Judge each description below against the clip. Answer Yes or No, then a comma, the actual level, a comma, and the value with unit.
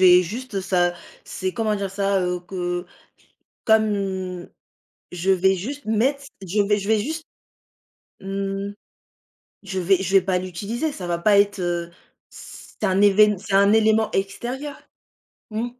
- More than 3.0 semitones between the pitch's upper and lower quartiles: No, narrow, 2.6 semitones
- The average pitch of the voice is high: Yes, high, 195 Hz